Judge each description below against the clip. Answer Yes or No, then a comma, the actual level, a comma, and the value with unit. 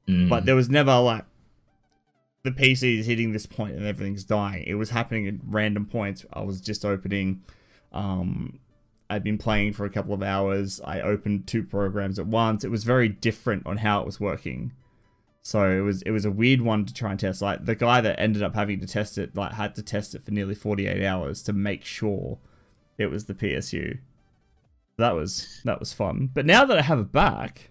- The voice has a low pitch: Yes, low, 105 Hz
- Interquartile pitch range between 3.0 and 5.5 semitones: No, narrow, 2.4 semitones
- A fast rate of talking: Yes, fast, 210 wpm